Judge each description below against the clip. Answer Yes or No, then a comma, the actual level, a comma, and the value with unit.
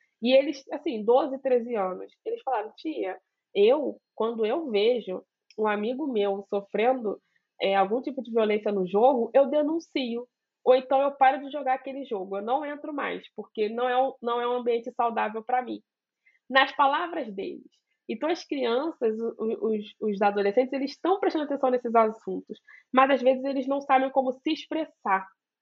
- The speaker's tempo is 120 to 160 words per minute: No, average, 170 wpm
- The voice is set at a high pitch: Yes, very high, 255 Hz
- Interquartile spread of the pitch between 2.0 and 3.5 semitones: No, average, 4.0 semitones